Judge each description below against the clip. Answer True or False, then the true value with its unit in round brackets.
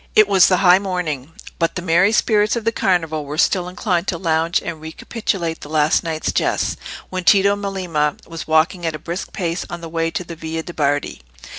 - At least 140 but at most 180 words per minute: False (205 wpm)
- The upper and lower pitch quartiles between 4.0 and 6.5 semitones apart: False (2.9 semitones)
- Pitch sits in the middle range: True (170 Hz)